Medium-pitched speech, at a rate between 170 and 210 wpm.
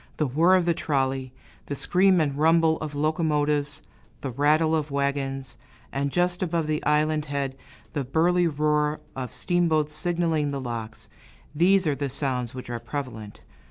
No: medium, 150 Hz; average, 160 wpm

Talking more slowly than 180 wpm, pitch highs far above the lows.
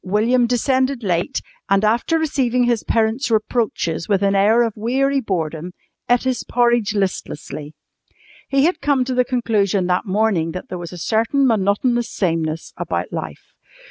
No: average, 160 wpm; average, 4.8 semitones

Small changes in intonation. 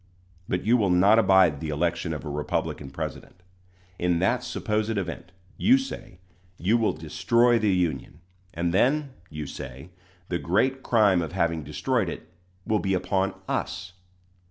No: average, 4.7 semitones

